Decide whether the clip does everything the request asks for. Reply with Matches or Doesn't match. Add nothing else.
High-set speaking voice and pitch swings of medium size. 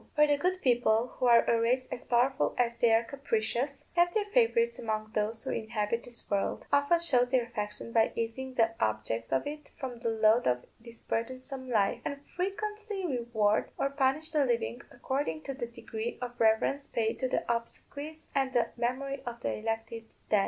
Matches